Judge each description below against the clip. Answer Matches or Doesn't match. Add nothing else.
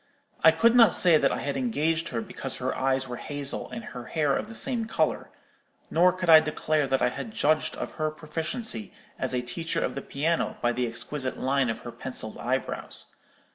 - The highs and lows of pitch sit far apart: Doesn't match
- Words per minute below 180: Doesn't match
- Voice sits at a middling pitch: Matches